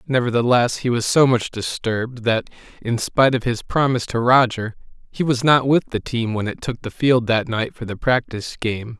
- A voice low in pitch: Yes, low, 120 Hz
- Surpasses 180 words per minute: Yes, fast, 205 wpm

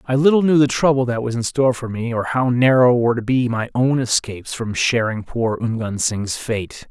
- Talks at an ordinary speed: No, fast, 225 wpm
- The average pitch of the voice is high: No, low, 120 Hz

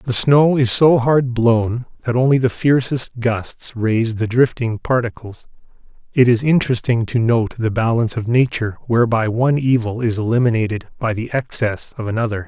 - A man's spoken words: Yes, male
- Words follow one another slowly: No, average, 160 wpm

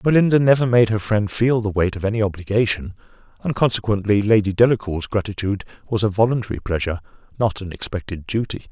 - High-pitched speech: No, low, 105 Hz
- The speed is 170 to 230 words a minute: No, average, 160 wpm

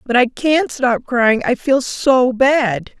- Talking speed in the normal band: Yes, average, 180 wpm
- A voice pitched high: Yes, very high, 255 Hz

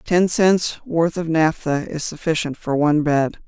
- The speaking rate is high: No, average, 175 wpm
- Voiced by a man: No, female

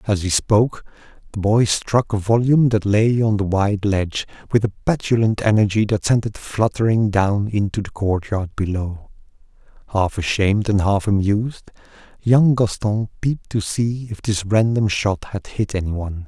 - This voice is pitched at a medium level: No, low, 105 Hz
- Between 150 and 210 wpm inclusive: Yes, average, 170 wpm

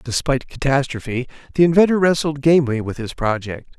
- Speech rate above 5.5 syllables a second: Yes, 5.9 syllables/s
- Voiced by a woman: No, male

